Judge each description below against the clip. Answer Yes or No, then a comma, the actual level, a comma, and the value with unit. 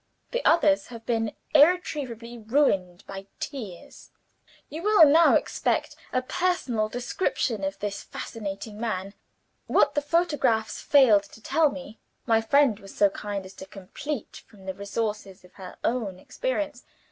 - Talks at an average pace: Yes, average, 145 wpm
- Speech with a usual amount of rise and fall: No, wide, 6.4 semitones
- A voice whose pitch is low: No, high, 225 Hz